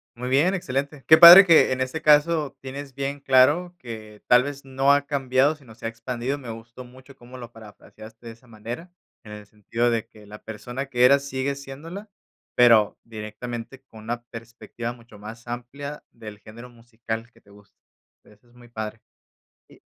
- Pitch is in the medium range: No, low, 125 Hz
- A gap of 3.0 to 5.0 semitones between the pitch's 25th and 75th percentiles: Yes, average, 3.5 semitones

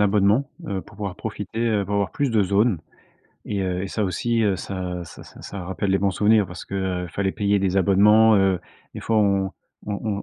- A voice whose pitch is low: Yes, low, 100 Hz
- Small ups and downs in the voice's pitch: Yes, narrow, 1.8 semitones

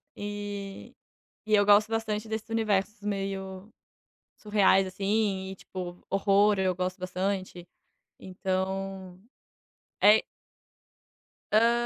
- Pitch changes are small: Yes, narrow, 1.7 semitones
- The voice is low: No, high, 195 Hz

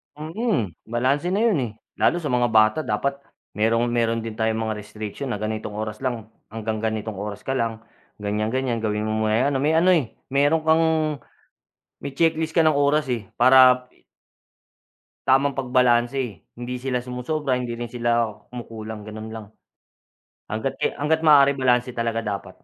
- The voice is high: No, low, 120 Hz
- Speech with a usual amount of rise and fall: Yes, average, 3.9 semitones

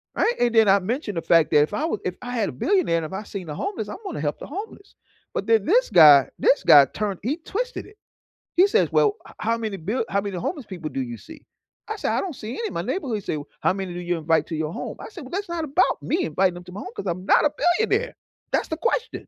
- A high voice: Yes, high, 215 Hz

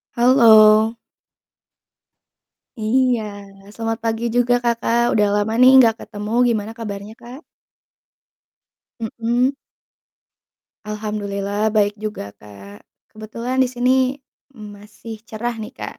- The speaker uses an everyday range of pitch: No, narrow, 2.1 semitones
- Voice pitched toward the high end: Yes, high, 220 Hz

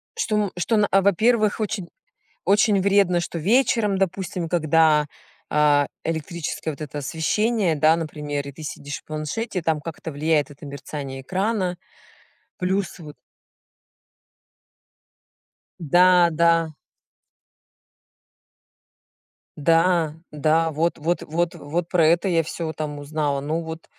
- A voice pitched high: No, medium, 165 Hz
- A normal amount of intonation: Yes, average, 3.5 semitones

